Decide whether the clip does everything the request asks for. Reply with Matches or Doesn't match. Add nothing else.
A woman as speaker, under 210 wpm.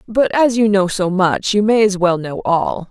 Doesn't match